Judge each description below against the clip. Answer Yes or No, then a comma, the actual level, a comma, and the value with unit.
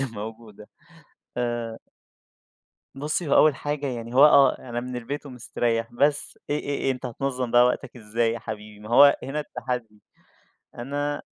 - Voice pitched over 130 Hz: No, low, 125 Hz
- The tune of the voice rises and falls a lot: No, average, 3.4 semitones